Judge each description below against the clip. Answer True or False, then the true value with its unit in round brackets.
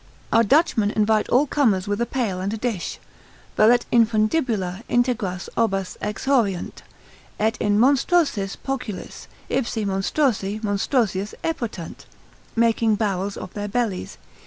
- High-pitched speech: True (215 Hz)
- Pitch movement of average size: True (3.5 semitones)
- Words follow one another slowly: True (120 wpm)